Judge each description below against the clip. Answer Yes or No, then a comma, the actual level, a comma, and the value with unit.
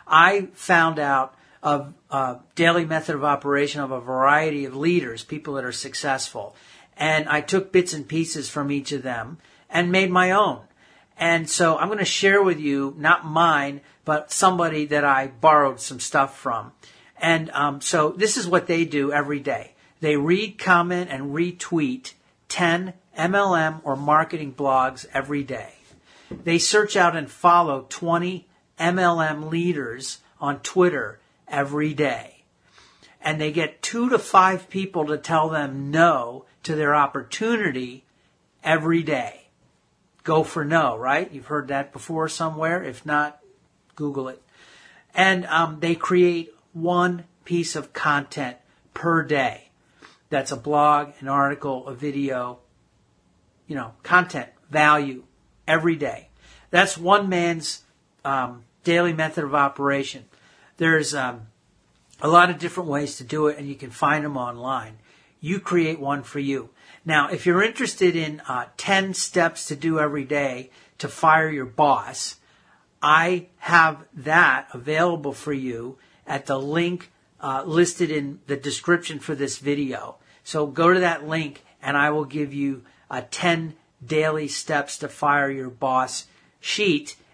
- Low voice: No, medium, 155 Hz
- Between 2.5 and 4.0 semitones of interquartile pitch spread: Yes, average, 3.4 semitones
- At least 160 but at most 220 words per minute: No, average, 150 wpm